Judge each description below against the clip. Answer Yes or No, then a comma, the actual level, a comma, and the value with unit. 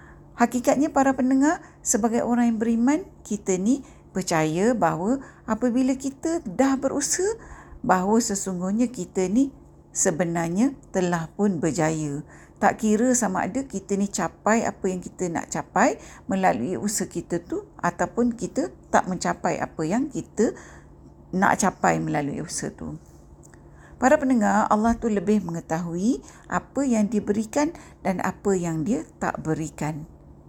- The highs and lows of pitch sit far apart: Yes, wide, 6.8 semitones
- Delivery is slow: No, average, 130 wpm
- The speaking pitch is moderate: No, high, 205 Hz